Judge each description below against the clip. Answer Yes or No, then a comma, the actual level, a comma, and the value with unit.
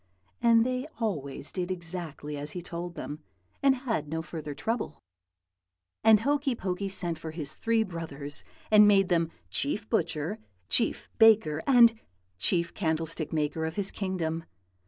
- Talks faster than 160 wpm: No, average, 145 wpm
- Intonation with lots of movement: Yes, wide, 5.7 semitones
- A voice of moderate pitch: Yes, medium, 175 Hz